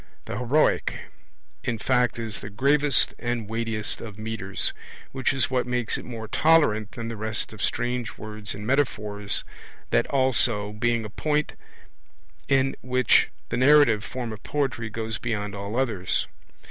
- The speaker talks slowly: No, average, 150 wpm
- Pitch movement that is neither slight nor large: Yes, average, 3.3 semitones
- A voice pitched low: Yes, low, 115 Hz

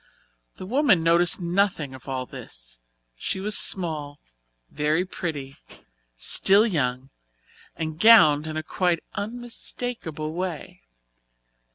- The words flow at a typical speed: No, slow, 105 wpm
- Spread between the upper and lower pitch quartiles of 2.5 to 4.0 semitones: No, average, 5.0 semitones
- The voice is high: No, medium, 165 Hz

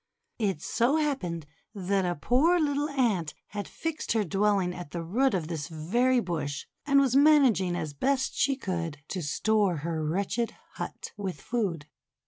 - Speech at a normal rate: Yes, average, 160 wpm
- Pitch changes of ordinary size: No, wide, 7.3 semitones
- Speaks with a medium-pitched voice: No, high, 200 Hz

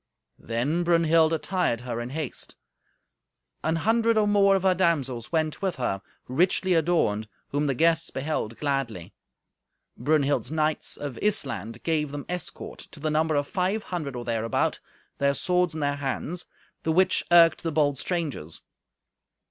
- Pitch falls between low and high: Yes, medium, 155 Hz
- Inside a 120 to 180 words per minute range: Yes, average, 150 wpm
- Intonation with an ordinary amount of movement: Yes, average, 4.5 semitones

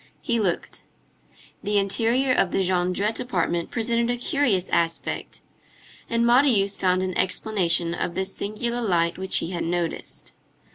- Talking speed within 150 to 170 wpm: No, average, 140 wpm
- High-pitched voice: Yes, high, 195 Hz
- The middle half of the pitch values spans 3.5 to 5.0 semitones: Yes, average, 4.7 semitones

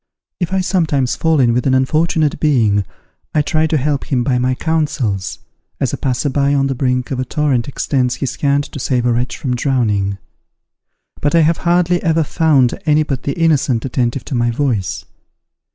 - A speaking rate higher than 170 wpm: Yes, average, 190 wpm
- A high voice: No, low, 135 Hz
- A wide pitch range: No, average, 3.7 semitones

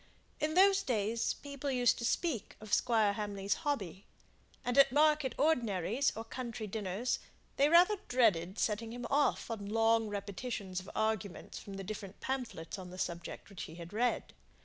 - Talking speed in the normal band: Yes, average, 165 wpm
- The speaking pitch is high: Yes, high, 225 Hz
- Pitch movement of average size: Yes, average, 4.4 semitones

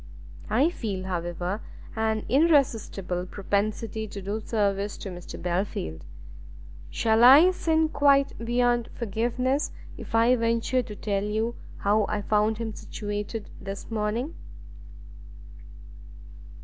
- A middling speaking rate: No, slow, 110 wpm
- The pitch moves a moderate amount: Yes, average, 3.2 semitones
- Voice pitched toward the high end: Yes, high, 220 Hz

